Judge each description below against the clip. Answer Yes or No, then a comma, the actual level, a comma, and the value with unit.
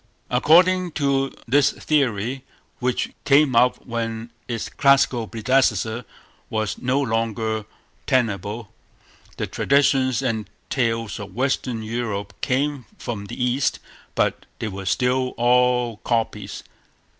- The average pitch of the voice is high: No, low, 120 Hz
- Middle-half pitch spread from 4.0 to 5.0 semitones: No, average, 3.2 semitones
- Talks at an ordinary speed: No, slow, 110 wpm